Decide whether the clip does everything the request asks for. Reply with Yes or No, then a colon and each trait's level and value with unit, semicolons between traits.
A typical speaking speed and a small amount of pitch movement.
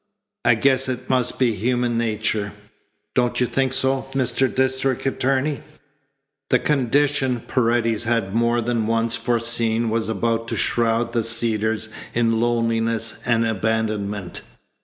No: slow, 130 wpm; narrow, 2.0 semitones